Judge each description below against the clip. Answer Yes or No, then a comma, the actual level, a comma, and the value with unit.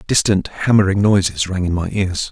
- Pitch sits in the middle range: No, very low, 95 Hz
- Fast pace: No, average, 180 wpm